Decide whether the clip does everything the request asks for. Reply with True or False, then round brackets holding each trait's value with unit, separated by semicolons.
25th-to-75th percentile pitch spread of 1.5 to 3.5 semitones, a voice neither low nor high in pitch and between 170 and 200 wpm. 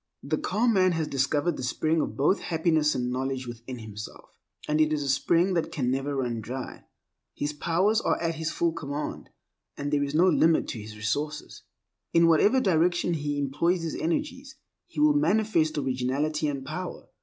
False (4.0 semitones; 150 Hz; 180 wpm)